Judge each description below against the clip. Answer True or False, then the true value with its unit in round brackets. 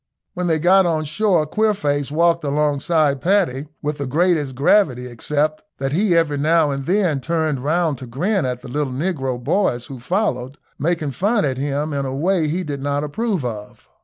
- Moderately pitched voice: True (150 Hz)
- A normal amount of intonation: True (4.1 semitones)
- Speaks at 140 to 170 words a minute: False (185 wpm)